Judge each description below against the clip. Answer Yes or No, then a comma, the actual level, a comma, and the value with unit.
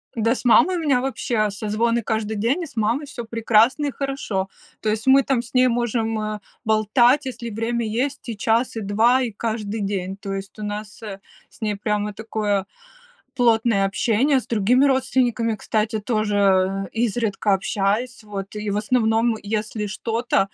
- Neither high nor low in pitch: No, high, 225 Hz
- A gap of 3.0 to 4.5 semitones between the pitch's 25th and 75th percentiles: No, narrow, 2.6 semitones